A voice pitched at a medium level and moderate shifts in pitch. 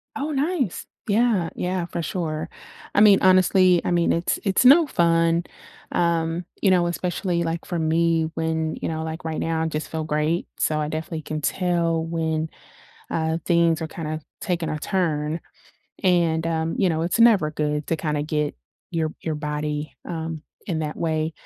No: medium, 165 Hz; narrow, 2.0 semitones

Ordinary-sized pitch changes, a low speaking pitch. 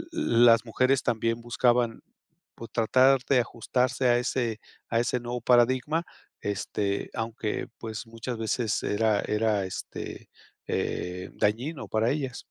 No: narrow, 2.0 semitones; low, 115 Hz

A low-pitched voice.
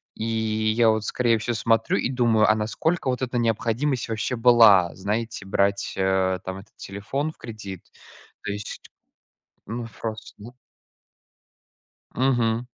Yes: low, 110 Hz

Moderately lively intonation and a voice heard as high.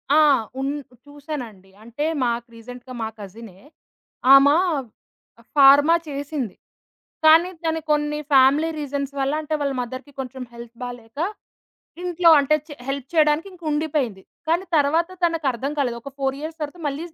Yes: average, 3.7 semitones; very high, 280 Hz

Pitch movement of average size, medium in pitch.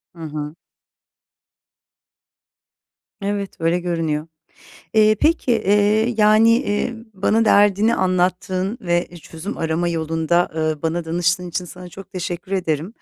Yes: average, 3.8 semitones; medium, 180 Hz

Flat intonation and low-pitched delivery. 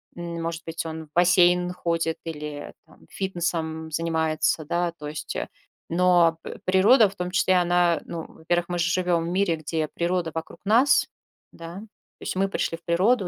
No: narrow, 1.7 semitones; medium, 170 Hz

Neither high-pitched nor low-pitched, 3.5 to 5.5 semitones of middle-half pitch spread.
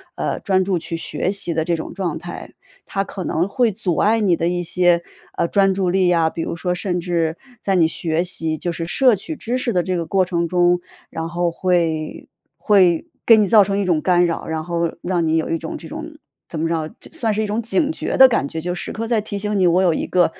No: medium, 180 Hz; average, 3.1 semitones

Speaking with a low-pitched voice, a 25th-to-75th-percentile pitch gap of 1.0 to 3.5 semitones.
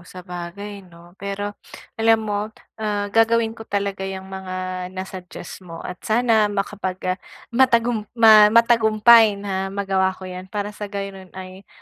No: high, 200 Hz; narrow, 2.5 semitones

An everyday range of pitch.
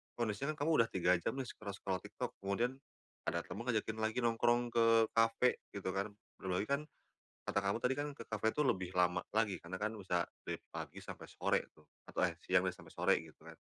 Yes: average, 4.3 semitones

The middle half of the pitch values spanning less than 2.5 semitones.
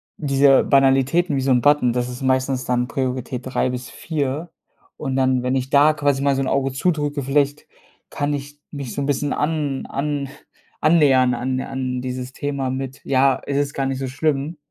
Yes: narrow, 1.8 semitones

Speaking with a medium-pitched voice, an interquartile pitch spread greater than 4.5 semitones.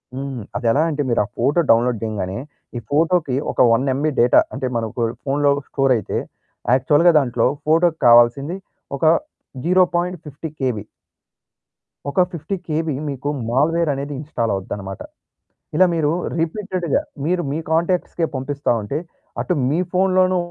Yes: medium, 145 Hz; average, 5.1 semitones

